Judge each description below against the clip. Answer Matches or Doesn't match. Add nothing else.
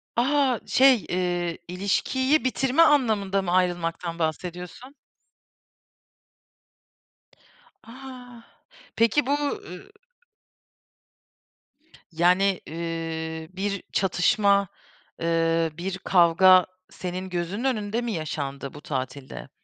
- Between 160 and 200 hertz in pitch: Matches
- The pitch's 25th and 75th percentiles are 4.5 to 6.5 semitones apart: Matches